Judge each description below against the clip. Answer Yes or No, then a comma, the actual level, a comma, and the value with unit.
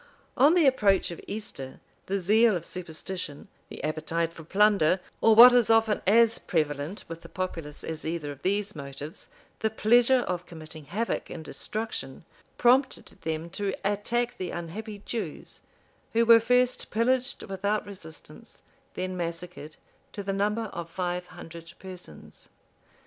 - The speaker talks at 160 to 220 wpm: No, average, 145 wpm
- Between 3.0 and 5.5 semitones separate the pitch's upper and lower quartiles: Yes, average, 5.1 semitones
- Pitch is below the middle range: No, high, 190 Hz